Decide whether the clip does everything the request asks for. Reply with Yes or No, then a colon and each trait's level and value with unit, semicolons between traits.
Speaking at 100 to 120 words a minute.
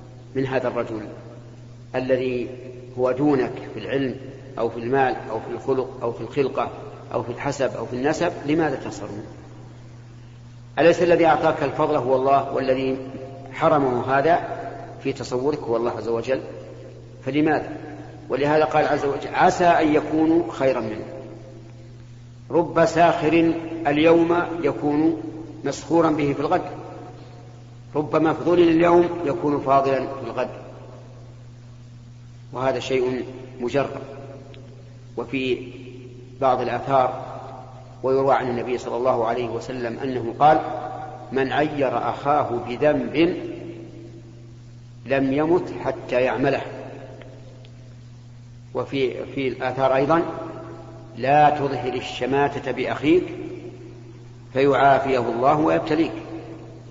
Yes: average, 105 wpm